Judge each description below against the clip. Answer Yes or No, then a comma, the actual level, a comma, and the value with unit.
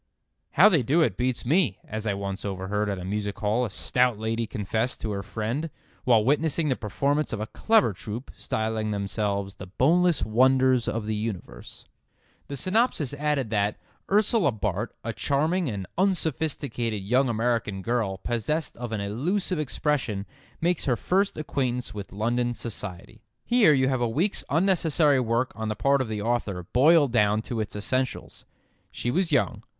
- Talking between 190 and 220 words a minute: No, average, 165 wpm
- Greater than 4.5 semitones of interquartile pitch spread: Yes, wide, 5.6 semitones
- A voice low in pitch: Yes, low, 120 Hz